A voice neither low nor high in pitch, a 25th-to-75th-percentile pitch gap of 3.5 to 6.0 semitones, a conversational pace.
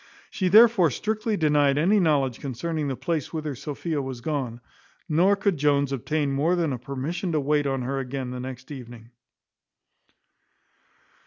Yes: medium, 145 Hz; average, 4.1 semitones; average, 155 wpm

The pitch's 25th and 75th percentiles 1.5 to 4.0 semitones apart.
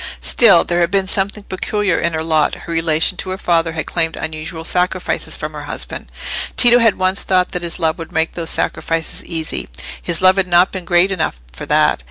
Yes: narrow, 2.5 semitones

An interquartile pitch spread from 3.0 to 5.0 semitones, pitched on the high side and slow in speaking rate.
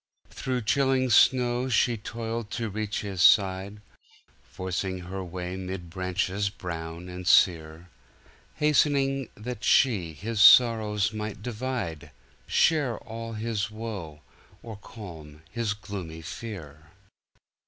No: average, 4.4 semitones; low, 105 Hz; slow, 110 wpm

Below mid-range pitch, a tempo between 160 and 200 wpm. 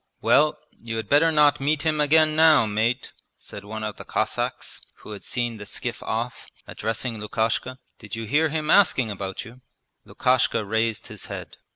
Yes: low, 120 Hz; average, 175 wpm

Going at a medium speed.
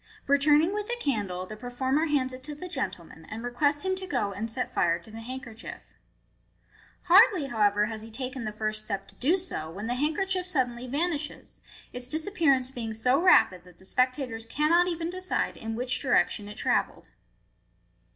Yes: average, 180 wpm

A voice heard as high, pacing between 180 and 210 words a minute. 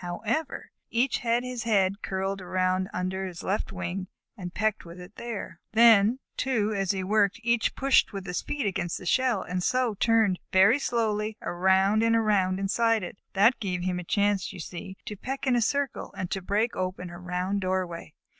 Yes: high, 195 Hz; average, 190 wpm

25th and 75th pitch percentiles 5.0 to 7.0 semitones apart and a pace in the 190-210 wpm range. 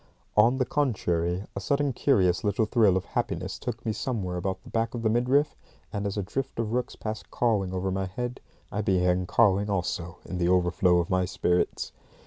No: average, 4.2 semitones; average, 195 wpm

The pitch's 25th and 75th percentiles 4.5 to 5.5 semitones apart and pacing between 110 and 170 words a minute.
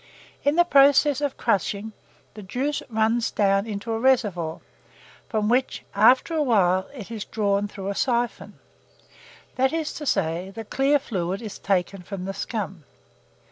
Yes: average, 5.0 semitones; average, 155 wpm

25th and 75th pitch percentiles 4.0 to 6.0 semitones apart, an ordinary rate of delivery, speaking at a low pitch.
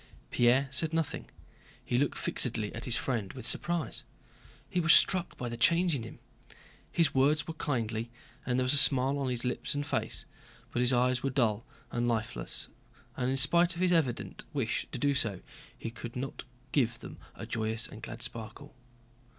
No: average, 3.6 semitones; average, 185 wpm; low, 125 Hz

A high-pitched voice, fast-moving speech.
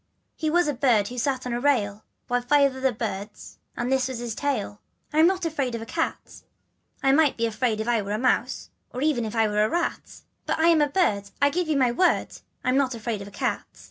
Yes: very high, 250 Hz; fast, 260 wpm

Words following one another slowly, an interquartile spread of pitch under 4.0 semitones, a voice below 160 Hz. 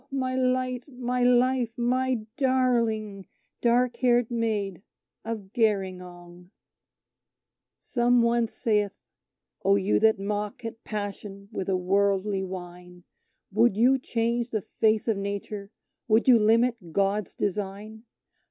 No: slow, 115 wpm; average, 3.4 semitones; high, 220 Hz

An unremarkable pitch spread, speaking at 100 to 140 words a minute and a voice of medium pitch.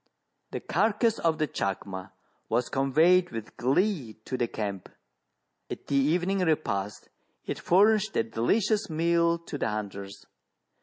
No: wide, 8.4 semitones; slow, 135 wpm; medium, 155 Hz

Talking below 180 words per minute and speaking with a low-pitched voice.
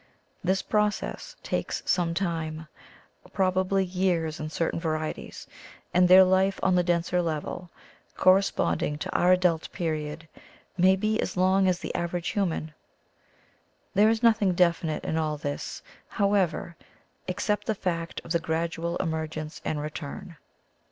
No: average, 140 wpm; medium, 175 Hz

